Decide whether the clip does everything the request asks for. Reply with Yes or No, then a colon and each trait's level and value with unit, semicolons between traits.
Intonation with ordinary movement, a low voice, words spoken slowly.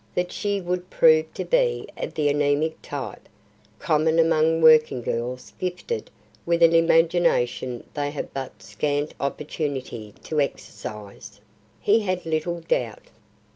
No: average, 3.2 semitones; medium, 155 Hz; slow, 130 wpm